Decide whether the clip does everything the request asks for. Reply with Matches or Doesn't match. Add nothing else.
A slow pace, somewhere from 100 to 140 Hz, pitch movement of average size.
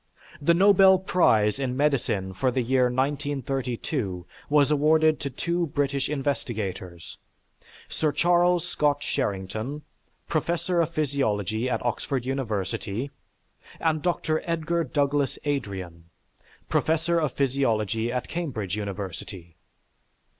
Doesn't match